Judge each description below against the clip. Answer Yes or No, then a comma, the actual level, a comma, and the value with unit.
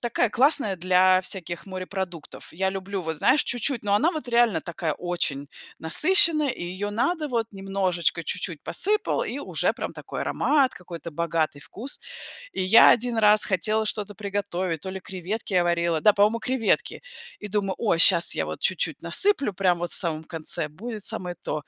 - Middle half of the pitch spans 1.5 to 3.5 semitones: No, average, 4.8 semitones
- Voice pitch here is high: Yes, high, 195 Hz